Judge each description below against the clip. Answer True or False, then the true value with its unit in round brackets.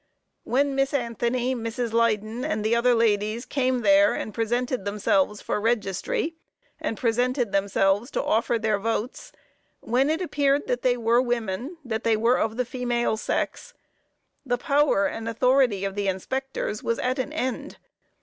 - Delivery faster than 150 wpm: True (160 wpm)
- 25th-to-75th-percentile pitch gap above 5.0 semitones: False (2.9 semitones)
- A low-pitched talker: False (235 Hz)